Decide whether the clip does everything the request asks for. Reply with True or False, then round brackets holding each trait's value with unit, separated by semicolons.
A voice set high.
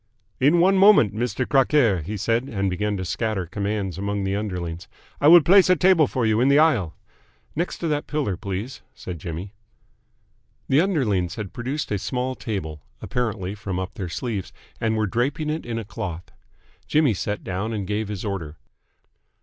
False (110 Hz)